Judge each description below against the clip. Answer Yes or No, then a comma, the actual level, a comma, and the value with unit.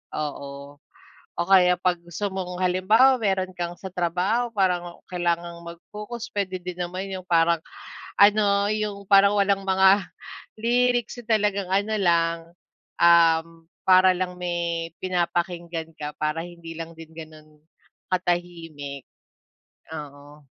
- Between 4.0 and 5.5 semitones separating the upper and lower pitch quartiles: No, average, 2.8 semitones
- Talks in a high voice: No, medium, 180 Hz